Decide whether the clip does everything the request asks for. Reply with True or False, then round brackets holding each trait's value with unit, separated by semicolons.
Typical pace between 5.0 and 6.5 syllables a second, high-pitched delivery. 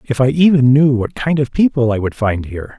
False (5.6 syllables/s; 130 Hz)